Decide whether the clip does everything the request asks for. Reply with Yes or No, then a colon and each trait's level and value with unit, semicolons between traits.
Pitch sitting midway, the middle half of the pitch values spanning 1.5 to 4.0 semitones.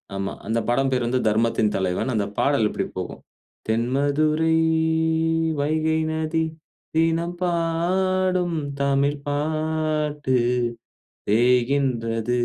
No: medium, 145 Hz; average, 4.7 semitones